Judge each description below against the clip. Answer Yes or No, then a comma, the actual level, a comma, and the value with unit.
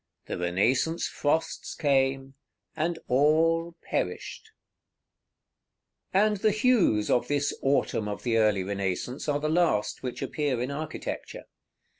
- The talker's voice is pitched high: No, medium, 140 Hz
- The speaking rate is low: Yes, slow, 130 wpm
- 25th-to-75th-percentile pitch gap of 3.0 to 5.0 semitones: No, wide, 5.6 semitones